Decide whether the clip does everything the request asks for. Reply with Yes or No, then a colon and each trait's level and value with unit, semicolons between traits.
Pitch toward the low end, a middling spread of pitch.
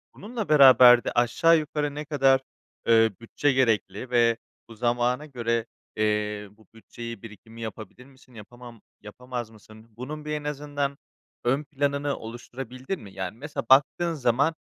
Yes: low, 125 Hz; average, 4.0 semitones